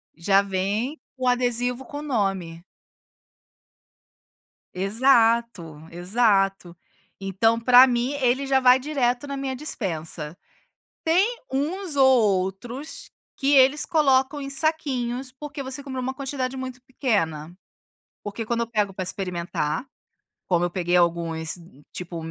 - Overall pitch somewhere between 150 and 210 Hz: No, high, 245 Hz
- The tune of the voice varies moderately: No, wide, 6.0 semitones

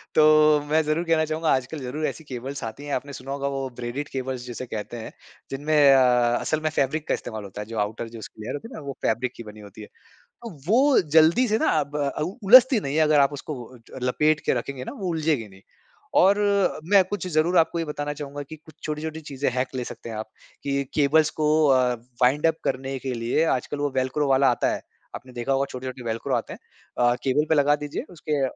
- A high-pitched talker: No, medium, 140 Hz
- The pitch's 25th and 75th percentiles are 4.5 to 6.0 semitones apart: No, average, 3.7 semitones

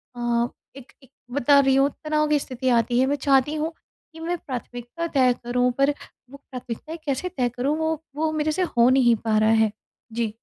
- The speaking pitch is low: No, very high, 265 Hz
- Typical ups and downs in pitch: Yes, average, 3.8 semitones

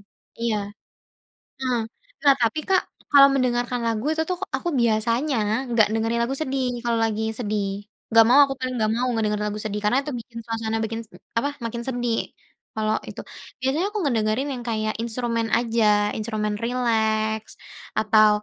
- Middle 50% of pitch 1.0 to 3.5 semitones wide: Yes, average, 2.7 semitones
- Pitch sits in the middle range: No, high, 230 Hz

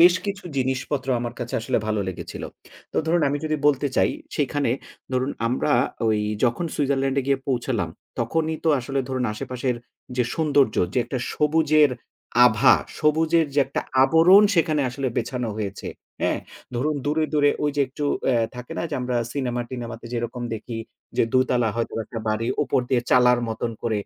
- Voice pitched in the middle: No, low, 130 Hz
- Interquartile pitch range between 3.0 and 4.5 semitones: Yes, average, 3.7 semitones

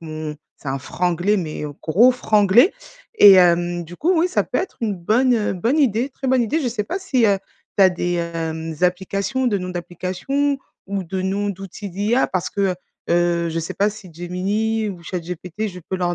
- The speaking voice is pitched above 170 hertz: Yes, high, 190 Hz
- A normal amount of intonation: Yes, average, 4.3 semitones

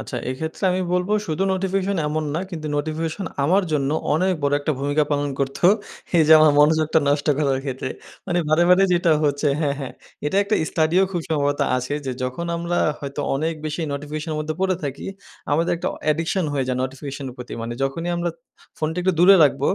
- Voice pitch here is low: No, medium, 155 Hz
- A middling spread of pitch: Yes, average, 3.4 semitones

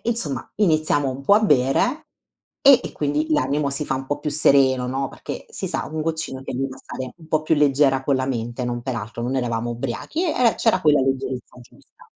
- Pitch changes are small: No, average, 3.1 semitones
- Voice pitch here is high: No, low, 135 Hz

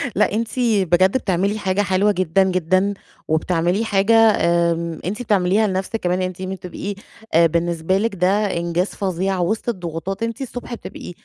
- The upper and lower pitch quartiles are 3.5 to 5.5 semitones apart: No, average, 3.0 semitones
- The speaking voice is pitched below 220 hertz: Yes, high, 190 Hz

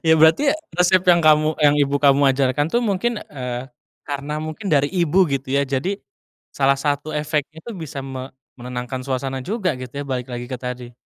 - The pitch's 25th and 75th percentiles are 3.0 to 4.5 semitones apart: Yes, average, 3.5 semitones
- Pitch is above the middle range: No, medium, 145 Hz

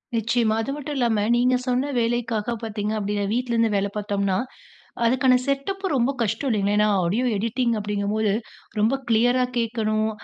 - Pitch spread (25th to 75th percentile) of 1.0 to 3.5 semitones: Yes, average, 3.0 semitones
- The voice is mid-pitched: No, high, 230 Hz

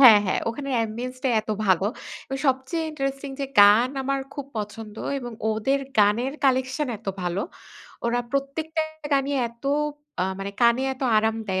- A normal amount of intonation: Yes, average, 4.1 semitones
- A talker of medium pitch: No, very high, 250 Hz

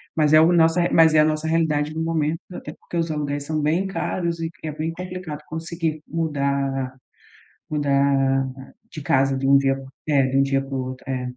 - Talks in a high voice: No, medium, 150 Hz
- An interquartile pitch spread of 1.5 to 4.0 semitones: Yes, average, 3.0 semitones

